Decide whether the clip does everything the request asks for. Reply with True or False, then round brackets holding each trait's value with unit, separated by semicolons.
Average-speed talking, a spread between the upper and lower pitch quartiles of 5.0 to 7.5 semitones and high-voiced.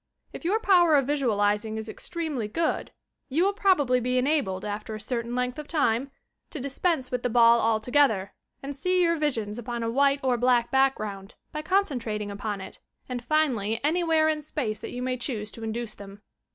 True (190 wpm; 5.5 semitones; 250 Hz)